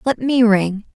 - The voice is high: Yes, high, 225 Hz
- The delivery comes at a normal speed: Yes, average, 185 wpm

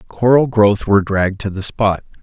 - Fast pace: No, average, 190 wpm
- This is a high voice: No, low, 105 Hz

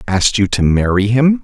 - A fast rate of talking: Yes, fast, 210 wpm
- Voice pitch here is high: No, low, 115 Hz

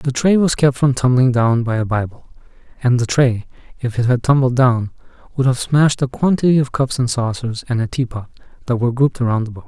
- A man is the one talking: Yes, male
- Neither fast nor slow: No, fast, 225 wpm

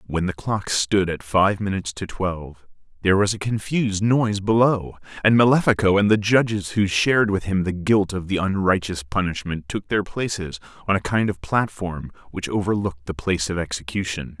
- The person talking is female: No, male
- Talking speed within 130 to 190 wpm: Yes, average, 185 wpm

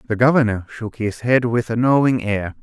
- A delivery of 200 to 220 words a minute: Yes, fast, 205 wpm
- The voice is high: No, low, 115 Hz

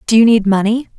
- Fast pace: Yes, fast, 245 wpm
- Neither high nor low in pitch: No, high, 220 Hz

